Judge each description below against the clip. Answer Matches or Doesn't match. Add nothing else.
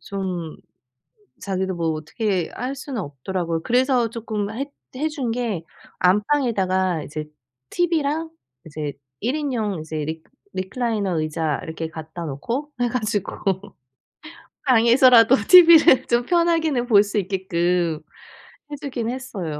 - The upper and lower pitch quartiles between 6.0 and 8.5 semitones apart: Matches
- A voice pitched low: Doesn't match